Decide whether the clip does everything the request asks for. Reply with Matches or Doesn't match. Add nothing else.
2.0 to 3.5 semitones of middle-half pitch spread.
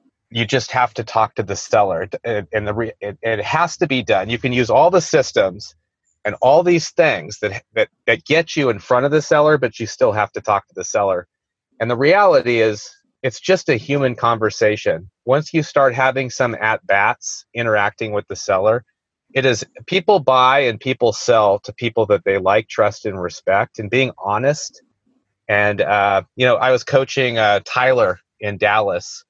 Doesn't match